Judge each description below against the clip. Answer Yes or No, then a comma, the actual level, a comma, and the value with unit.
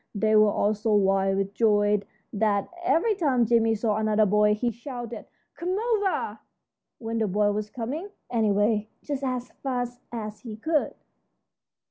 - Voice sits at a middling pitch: No, high, 220 Hz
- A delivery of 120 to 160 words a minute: Yes, average, 150 wpm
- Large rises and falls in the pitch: No, average, 3.1 semitones